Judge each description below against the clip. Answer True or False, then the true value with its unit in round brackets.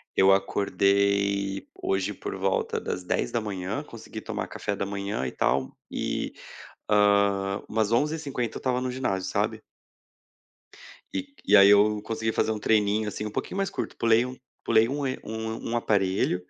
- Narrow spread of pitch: True (2.3 semitones)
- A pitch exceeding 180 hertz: False (105 Hz)